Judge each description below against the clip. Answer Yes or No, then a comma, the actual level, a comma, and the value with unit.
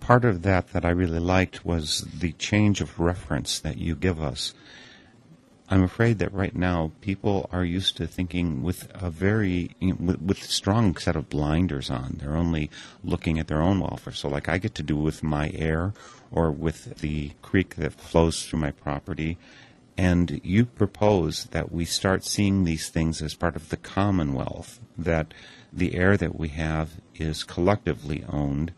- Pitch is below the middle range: Yes, very low, 85 Hz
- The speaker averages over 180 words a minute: No, average, 175 wpm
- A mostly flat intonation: No, average, 3.2 semitones